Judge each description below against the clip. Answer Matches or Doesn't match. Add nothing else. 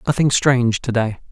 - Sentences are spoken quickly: Doesn't match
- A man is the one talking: Matches